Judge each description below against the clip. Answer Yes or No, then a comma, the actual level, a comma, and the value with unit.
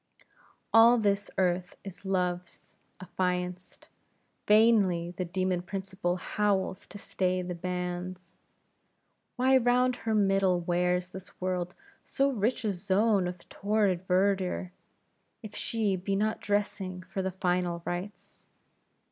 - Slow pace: Yes, slow, 120 wpm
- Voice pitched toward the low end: No, medium, 185 Hz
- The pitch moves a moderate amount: No, narrow, 2.3 semitones